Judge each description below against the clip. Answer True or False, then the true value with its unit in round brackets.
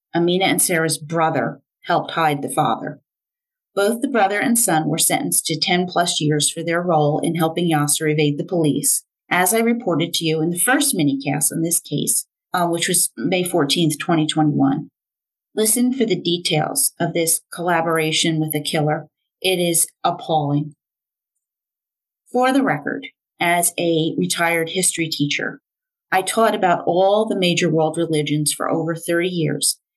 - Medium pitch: True (170 Hz)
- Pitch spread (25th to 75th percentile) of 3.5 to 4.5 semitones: False (2.6 semitones)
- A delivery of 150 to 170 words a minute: True (160 wpm)